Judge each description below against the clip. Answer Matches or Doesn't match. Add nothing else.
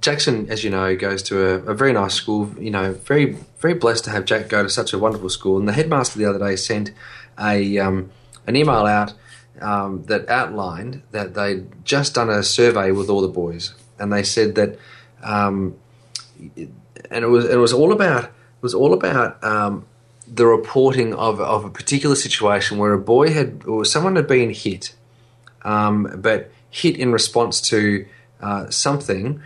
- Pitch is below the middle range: Matches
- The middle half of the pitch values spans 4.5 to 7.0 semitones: Doesn't match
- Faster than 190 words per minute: Doesn't match